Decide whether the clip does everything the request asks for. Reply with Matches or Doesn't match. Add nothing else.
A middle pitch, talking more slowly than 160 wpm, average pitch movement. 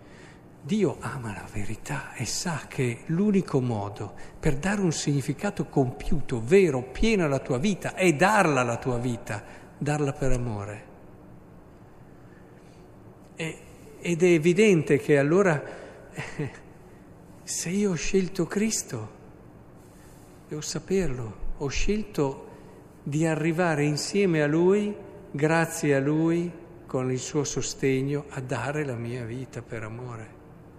Doesn't match